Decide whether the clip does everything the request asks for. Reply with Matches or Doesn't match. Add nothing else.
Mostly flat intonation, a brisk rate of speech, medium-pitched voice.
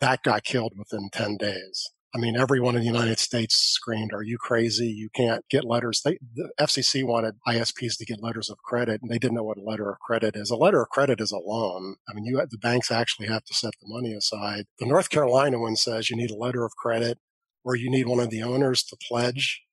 Doesn't match